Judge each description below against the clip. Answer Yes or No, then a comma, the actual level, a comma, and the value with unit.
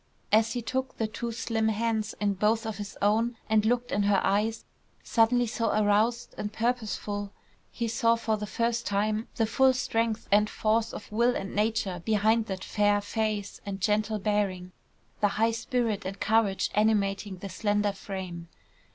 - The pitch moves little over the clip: Yes, narrow, 1.9 semitones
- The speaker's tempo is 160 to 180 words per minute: Yes, average, 165 wpm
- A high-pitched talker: Yes, high, 215 Hz